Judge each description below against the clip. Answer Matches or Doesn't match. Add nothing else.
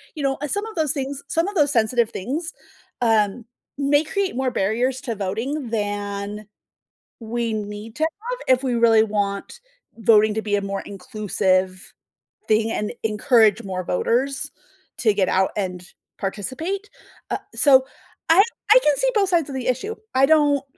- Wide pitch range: Matches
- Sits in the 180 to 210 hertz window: Doesn't match